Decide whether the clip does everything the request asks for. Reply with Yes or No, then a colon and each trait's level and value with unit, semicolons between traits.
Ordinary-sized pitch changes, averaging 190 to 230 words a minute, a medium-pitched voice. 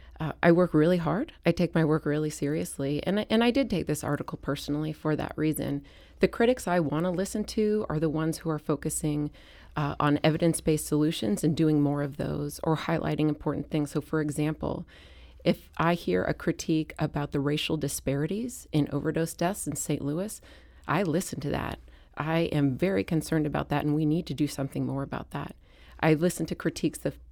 No: narrow, 2.3 semitones; average, 200 wpm; medium, 155 Hz